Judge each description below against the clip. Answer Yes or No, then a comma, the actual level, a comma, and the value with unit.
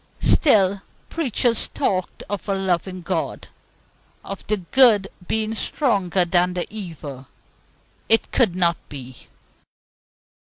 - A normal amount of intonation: Yes, average, 3.7 semitones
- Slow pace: Yes, slow, 110 wpm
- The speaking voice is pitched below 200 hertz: Yes, high, 190 Hz